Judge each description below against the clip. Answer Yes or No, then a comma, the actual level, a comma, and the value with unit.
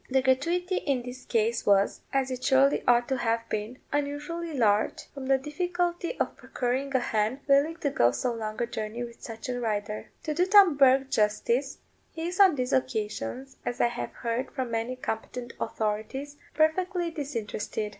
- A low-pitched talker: No, very high, 255 Hz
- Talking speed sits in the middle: Yes, average, 175 wpm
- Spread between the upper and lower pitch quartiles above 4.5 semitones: No, average, 4.2 semitones